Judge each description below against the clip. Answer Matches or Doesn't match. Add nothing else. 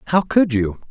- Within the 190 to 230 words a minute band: Matches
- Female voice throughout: Doesn't match